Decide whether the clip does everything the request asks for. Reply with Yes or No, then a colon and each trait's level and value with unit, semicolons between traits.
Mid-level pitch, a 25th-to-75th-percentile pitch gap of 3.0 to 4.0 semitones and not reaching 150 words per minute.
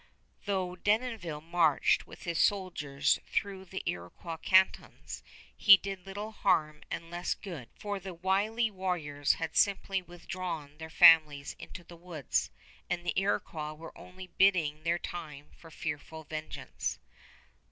Yes: medium, 175 Hz; average, 3.5 semitones; slow, 135 wpm